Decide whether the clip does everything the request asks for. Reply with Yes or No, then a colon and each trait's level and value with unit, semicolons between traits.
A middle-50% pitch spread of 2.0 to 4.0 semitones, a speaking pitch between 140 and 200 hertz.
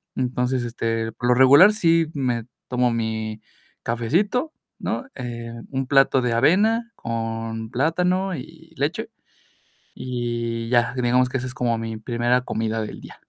No: average, 2.9 semitones; low, 125 Hz